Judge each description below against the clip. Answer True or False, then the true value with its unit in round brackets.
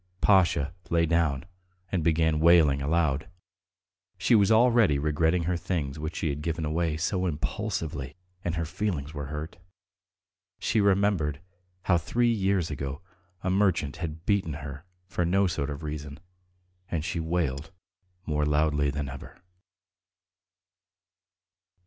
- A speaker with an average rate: False (130 wpm)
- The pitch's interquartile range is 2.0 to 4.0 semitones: True (3.5 semitones)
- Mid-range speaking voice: False (80 Hz)